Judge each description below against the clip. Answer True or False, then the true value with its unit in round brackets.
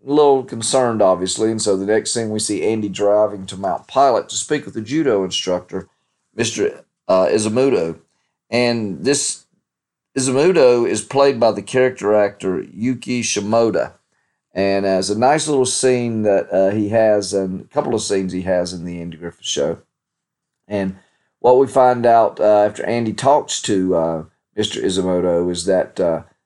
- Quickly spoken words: False (170 wpm)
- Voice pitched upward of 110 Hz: False (105 Hz)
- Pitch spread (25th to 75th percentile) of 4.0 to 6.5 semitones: True (4.7 semitones)